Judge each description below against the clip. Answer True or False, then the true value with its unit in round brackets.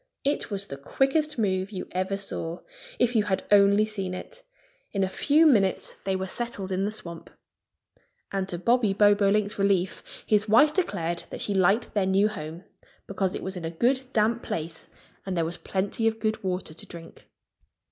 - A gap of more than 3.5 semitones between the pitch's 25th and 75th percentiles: False (2.8 semitones)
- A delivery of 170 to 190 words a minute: True (185 wpm)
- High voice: True (200 Hz)